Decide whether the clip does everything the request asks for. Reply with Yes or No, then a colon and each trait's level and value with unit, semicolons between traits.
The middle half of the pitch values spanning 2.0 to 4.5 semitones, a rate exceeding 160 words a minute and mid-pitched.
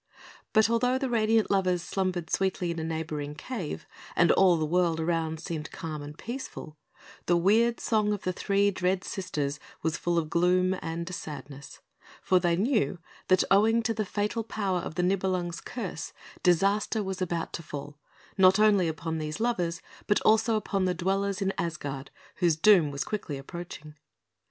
Yes: average, 3.9 semitones; average, 170 wpm; medium, 180 Hz